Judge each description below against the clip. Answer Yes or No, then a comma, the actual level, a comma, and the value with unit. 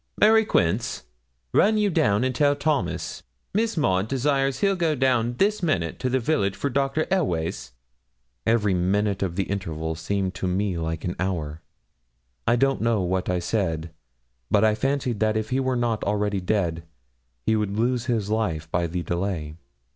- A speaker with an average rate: Yes, average, 170 wpm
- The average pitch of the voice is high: No, low, 105 Hz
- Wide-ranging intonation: Yes, wide, 6.6 semitones